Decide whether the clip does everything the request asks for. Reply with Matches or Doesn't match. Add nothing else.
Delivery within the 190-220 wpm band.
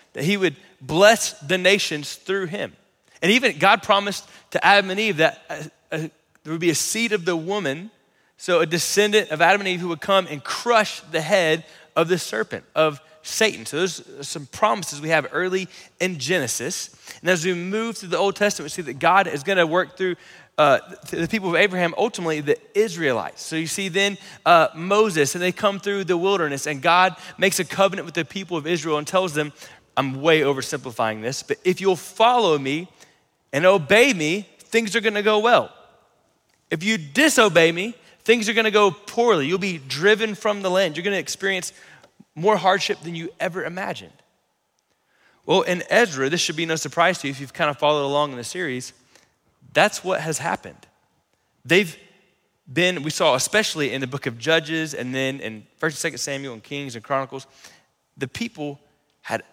Matches